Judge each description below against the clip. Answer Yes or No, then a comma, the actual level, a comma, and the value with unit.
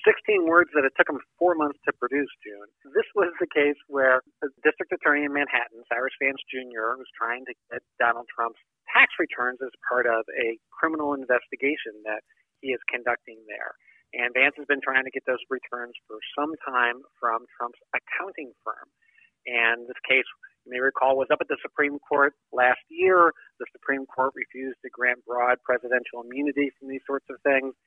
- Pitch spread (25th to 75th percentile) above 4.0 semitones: No, average, 2.9 semitones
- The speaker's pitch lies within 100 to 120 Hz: No, low, 135 Hz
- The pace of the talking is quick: No, average, 185 wpm